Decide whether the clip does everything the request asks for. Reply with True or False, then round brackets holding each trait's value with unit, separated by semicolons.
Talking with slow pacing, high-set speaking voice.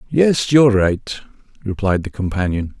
False (130 wpm; 105 Hz)